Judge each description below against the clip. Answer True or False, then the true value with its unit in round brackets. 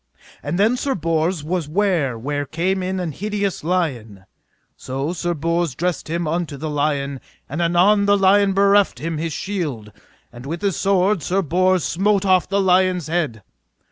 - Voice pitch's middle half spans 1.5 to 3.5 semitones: False (4.2 semitones)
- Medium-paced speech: True (170 wpm)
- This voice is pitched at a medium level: True (175 Hz)